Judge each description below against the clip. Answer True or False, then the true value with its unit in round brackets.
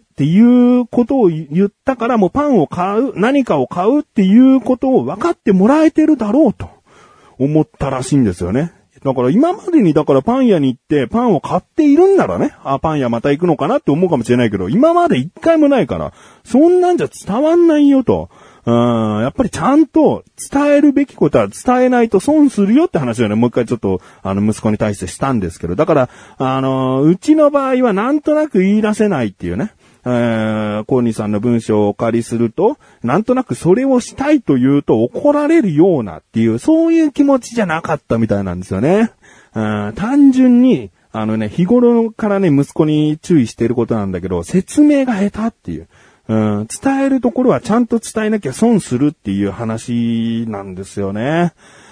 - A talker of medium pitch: True (180 Hz)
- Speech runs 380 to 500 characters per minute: True (400 characters per minute)